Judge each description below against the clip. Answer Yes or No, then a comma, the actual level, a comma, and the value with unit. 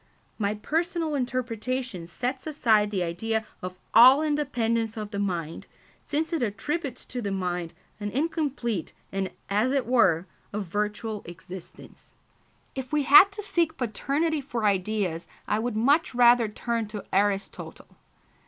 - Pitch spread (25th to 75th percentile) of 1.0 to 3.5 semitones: No, average, 5.2 semitones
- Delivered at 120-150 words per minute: Yes, average, 140 wpm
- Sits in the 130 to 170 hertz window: No, high, 225 Hz